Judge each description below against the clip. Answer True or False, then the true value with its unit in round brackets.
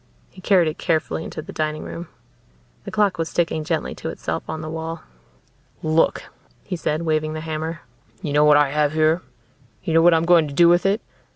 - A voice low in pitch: False (160 Hz)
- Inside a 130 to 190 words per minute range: False (205 wpm)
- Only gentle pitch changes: True (1.6 semitones)